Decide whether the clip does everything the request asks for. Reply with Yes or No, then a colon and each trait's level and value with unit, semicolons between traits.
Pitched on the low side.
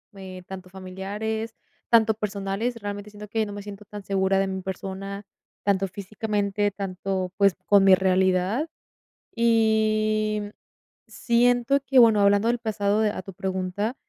No: high, 205 Hz